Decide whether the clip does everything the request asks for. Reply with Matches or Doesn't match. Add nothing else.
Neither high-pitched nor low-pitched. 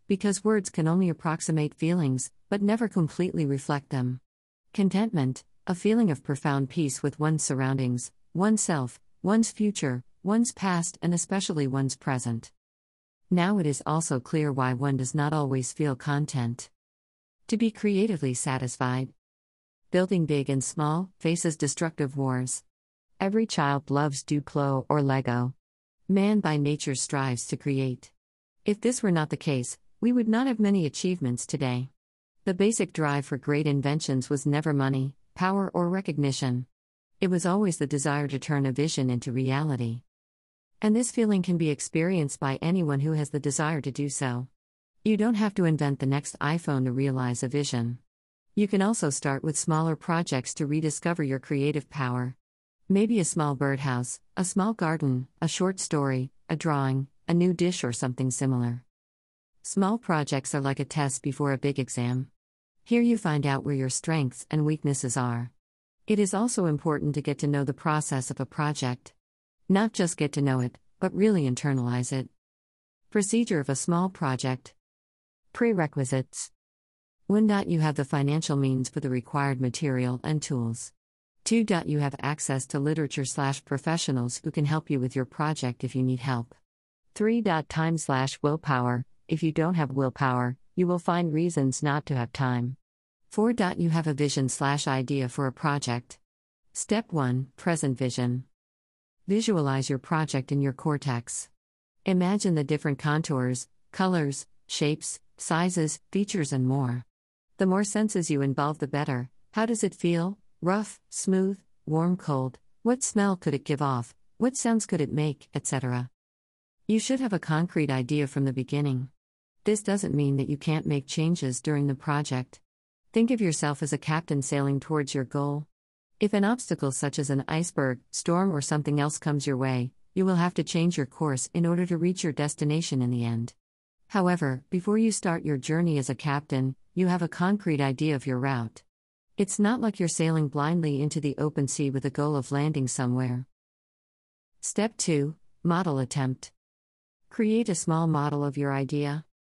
Matches